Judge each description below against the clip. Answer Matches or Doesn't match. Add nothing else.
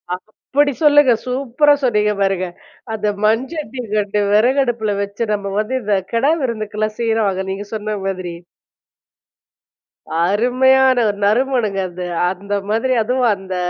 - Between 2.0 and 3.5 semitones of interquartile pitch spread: Doesn't match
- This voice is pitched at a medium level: Doesn't match